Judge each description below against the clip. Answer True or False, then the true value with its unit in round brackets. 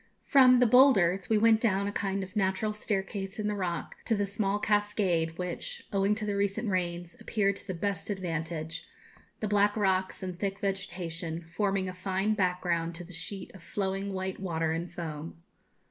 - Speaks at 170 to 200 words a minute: True (180 wpm)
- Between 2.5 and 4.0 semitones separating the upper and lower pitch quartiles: True (2.8 semitones)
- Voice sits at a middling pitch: False (195 Hz)